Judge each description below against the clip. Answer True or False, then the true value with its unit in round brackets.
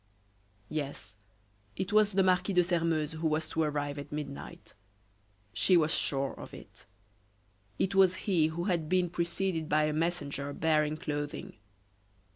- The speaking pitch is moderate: True (160 Hz)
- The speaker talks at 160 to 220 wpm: False (145 wpm)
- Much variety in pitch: False (3.2 semitones)